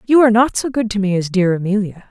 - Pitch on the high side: Yes, high, 210 Hz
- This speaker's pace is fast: Yes, fast, 285 wpm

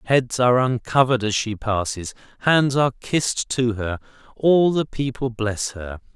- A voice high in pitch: No, low, 120 Hz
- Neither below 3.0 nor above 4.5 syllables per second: No, 4.7 syllables/s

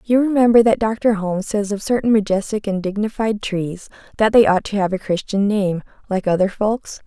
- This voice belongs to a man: No, female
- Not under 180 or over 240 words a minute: Yes, average, 195 wpm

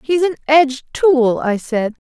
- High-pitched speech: Yes, very high, 270 Hz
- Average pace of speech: Yes, average, 175 wpm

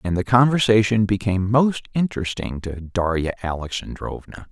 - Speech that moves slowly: Yes, slow, 120 wpm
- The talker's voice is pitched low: Yes, low, 105 Hz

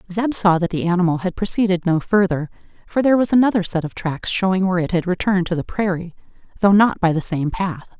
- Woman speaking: Yes, female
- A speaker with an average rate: No, fast, 220 wpm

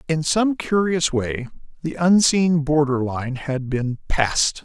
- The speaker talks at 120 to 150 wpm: Yes, average, 140 wpm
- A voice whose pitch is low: No, medium, 150 Hz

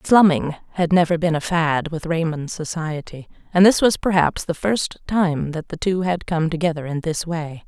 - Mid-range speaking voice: Yes, medium, 165 Hz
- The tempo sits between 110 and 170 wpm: No, average, 195 wpm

